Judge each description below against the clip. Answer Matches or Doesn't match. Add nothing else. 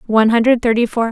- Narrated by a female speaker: Matches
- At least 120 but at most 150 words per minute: Doesn't match